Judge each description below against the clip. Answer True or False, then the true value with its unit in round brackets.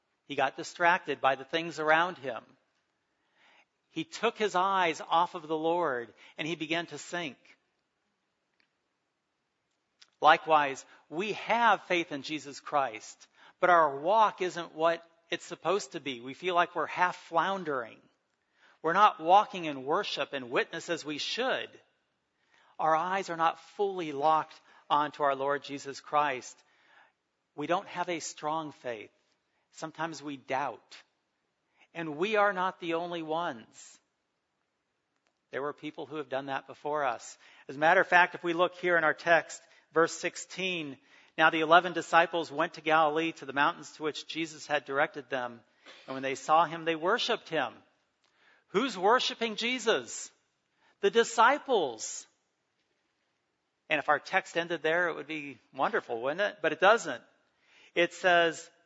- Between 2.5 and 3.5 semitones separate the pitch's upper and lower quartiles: True (2.9 semitones)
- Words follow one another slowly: False (150 wpm)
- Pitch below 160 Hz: False (165 Hz)